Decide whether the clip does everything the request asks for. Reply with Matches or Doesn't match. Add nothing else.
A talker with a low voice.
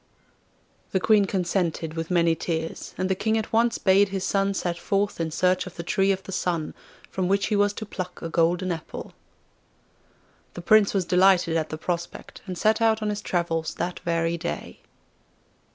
Doesn't match